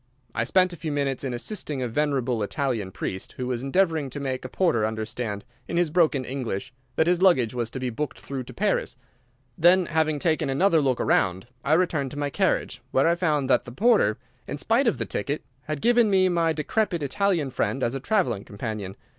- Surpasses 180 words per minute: Yes, fast, 205 wpm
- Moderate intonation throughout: No, wide, 5.7 semitones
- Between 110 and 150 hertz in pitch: Yes, medium, 140 Hz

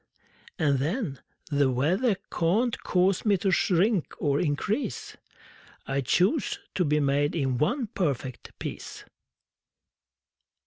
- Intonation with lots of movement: Yes, wide, 6.0 semitones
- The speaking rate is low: Yes, slow, 115 wpm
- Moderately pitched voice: Yes, medium, 165 Hz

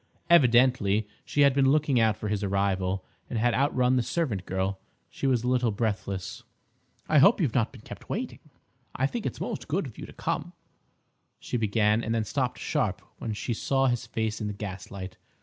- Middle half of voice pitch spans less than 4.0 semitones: No, average, 4.4 semitones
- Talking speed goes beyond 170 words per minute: Yes, average, 190 wpm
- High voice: No, low, 115 Hz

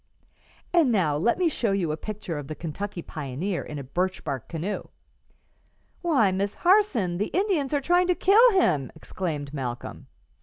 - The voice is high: Yes, high, 195 Hz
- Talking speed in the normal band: Yes, average, 165 wpm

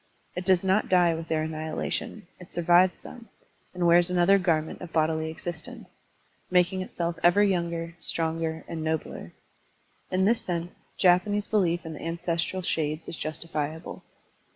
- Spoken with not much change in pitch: Yes, narrow, 2.3 semitones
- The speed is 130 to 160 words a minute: Yes, average, 145 wpm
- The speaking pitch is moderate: Yes, medium, 170 Hz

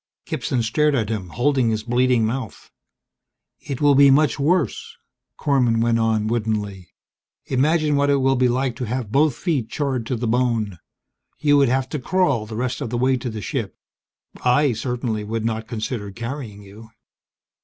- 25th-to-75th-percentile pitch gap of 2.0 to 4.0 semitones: Yes, average, 3.7 semitones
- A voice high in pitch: No, low, 125 Hz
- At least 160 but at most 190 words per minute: Yes, average, 175 wpm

